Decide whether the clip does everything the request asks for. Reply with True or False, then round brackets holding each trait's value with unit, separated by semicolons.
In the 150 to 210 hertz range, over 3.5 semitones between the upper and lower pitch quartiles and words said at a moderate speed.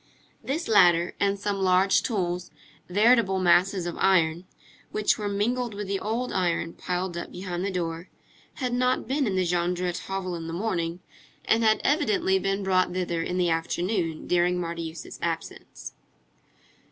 False (185 Hz; 3.0 semitones; 155 wpm)